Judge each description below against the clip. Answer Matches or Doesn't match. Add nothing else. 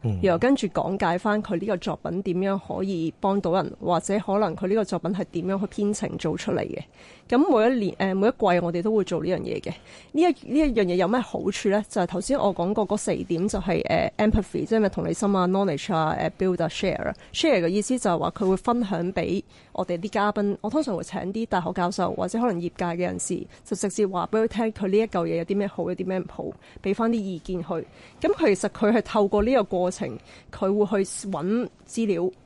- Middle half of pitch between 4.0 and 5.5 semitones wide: Doesn't match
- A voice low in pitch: Doesn't match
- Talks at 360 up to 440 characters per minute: Matches